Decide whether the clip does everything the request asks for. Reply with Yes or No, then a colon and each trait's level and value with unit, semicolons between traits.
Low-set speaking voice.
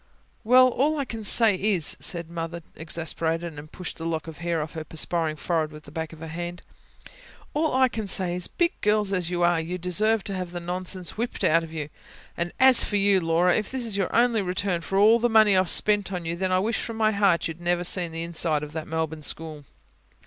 No: medium, 175 Hz